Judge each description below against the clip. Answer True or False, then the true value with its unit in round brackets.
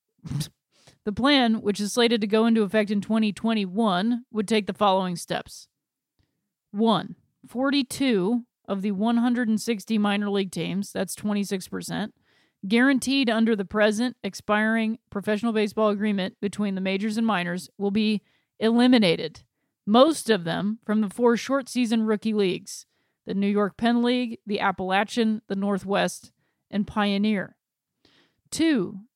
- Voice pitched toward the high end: True (215 Hz)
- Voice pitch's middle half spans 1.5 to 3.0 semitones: True (2.5 semitones)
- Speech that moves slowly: True (130 wpm)